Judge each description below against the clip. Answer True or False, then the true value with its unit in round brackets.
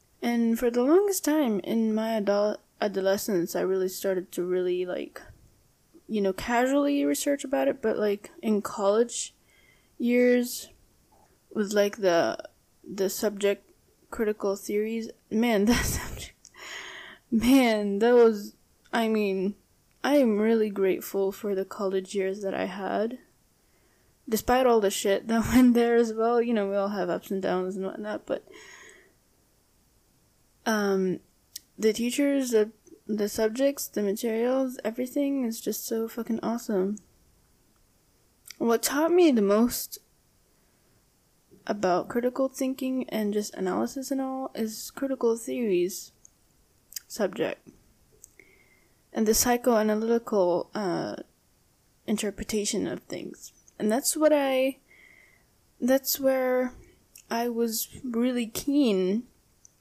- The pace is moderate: False (120 wpm)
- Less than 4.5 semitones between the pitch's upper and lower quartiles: True (3.7 semitones)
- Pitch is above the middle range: True (225 Hz)